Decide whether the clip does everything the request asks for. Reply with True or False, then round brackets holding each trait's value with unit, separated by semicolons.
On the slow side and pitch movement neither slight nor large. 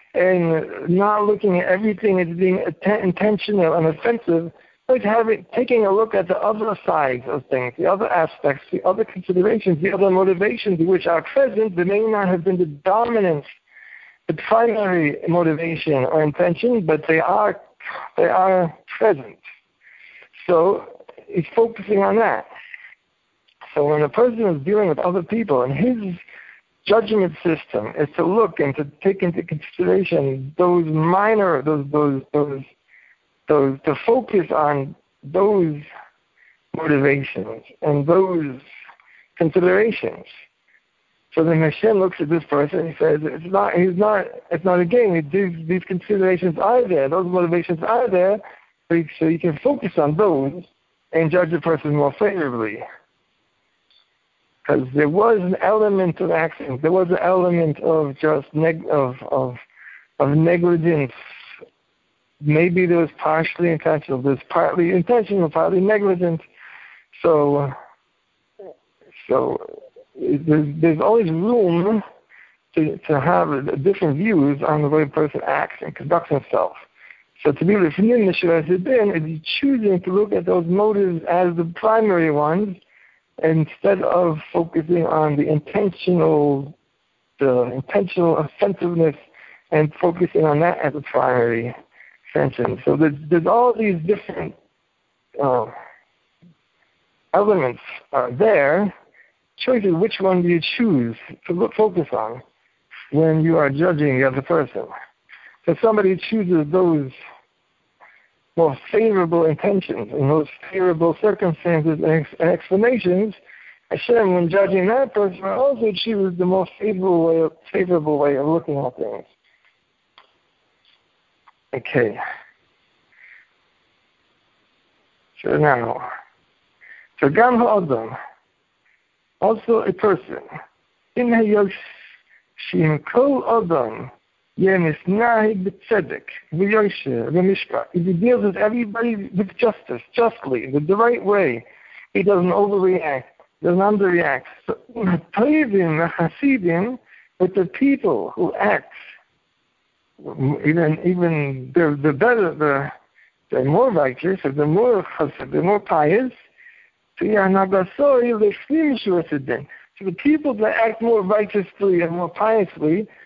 True (125 wpm; 4.7 semitones)